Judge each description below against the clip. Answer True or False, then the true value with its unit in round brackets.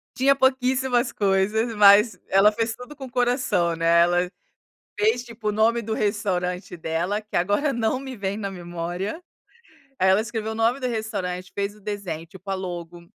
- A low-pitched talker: False (210 Hz)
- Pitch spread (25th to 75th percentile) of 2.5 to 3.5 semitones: False (4.4 semitones)